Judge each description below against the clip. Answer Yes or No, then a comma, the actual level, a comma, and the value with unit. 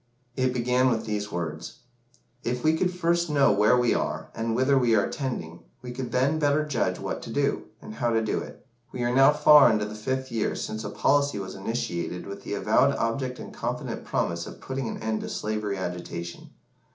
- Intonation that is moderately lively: Yes, average, 4.1 semitones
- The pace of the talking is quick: Yes, fast, 210 wpm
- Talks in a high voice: No, low, 120 Hz